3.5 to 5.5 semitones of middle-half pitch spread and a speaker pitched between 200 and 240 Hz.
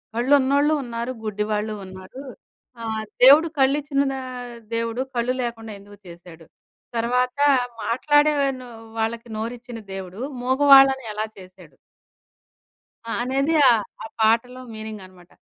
Yes: average, 3.8 semitones; high, 235 Hz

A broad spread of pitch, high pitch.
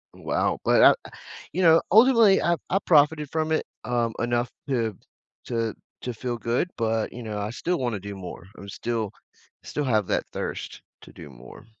No: wide, 6.3 semitones; low, 120 Hz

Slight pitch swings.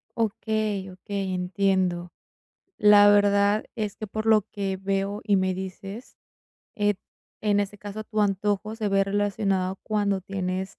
Yes: narrow, 1.5 semitones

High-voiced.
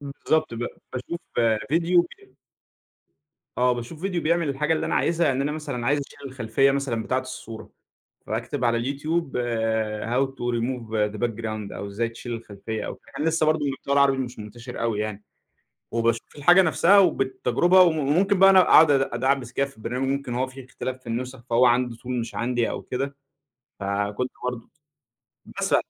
No: low, 130 Hz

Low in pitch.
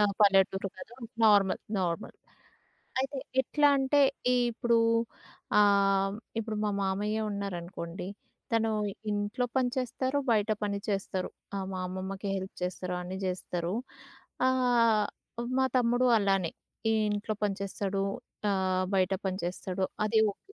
No: high, 200 Hz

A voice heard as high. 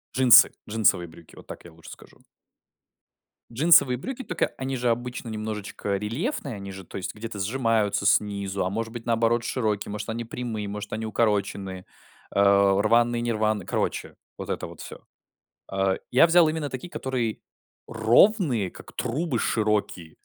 No: low, 110 Hz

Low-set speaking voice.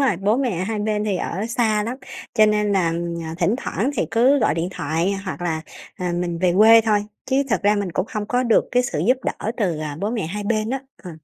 No: high, 210 Hz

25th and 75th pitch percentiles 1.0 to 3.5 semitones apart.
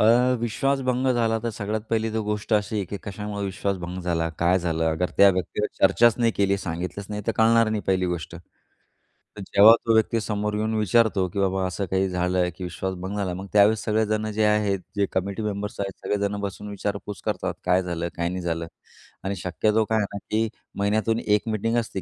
Yes: average, 2.8 semitones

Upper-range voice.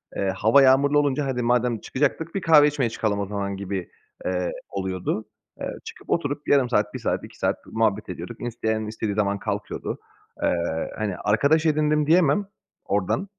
No: low, 115 Hz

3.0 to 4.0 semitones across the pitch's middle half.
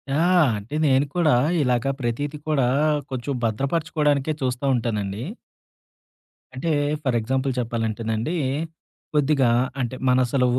Yes: average, 3.5 semitones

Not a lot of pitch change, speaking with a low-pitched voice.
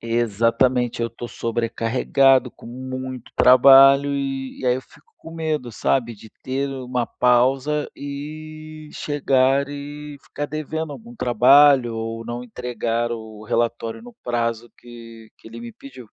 No: average, 3.2 semitones; low, 130 Hz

